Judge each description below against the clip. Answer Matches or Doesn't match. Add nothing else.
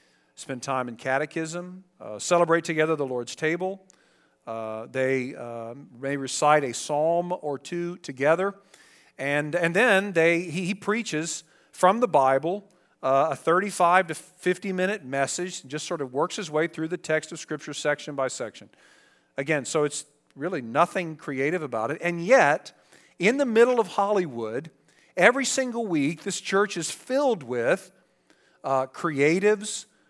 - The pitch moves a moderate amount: Matches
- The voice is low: Doesn't match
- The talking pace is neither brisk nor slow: Matches